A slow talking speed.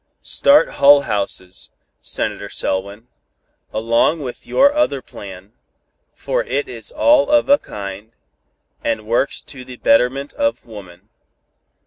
Yes: slow, 120 wpm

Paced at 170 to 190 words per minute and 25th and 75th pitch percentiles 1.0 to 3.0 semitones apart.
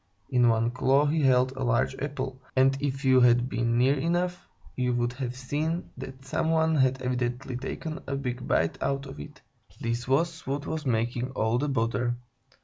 Yes: average, 185 wpm; narrow, 2.5 semitones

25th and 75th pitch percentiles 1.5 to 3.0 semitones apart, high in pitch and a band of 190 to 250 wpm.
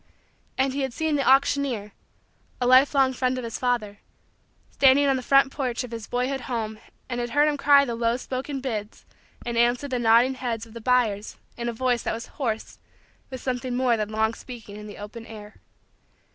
Yes: average, 2.7 semitones; high, 245 Hz; average, 200 wpm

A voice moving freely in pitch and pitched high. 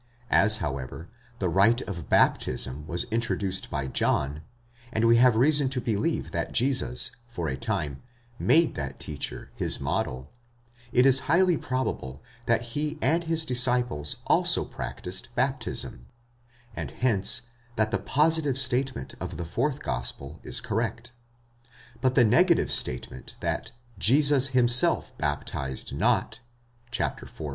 No: wide, 8.2 semitones; low, 115 Hz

